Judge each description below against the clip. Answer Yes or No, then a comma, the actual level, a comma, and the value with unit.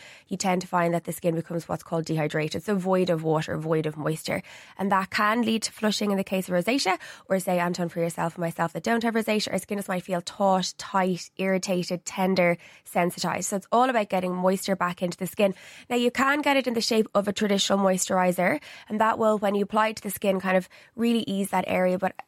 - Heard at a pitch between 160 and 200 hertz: Yes, high, 190 Hz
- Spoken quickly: Yes, fast, 240 wpm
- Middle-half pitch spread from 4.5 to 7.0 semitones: No, average, 3.2 semitones